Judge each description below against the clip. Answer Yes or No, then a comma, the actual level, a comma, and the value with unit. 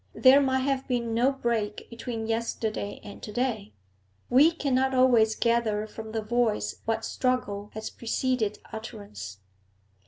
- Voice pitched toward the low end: No, high, 230 Hz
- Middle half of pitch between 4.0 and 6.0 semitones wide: No, average, 2.9 semitones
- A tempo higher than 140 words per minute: No, slow, 135 wpm